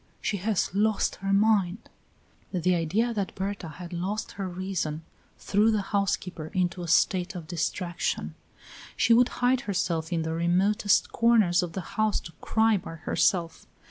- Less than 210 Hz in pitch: Yes, high, 190 Hz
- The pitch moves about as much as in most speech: Yes, average, 3.3 semitones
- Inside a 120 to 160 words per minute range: Yes, average, 155 wpm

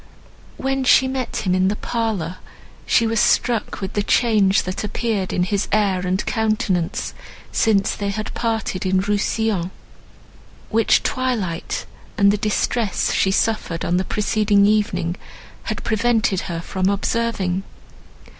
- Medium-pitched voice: No, high, 205 Hz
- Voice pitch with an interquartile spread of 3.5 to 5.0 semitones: No, average, 3.1 semitones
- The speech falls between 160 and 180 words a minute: No, slow, 135 wpm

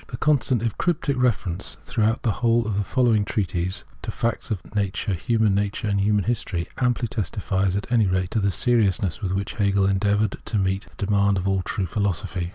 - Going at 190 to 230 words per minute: Yes, average, 200 wpm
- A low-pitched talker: Yes, low, 100 Hz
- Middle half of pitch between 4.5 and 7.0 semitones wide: No, average, 3.0 semitones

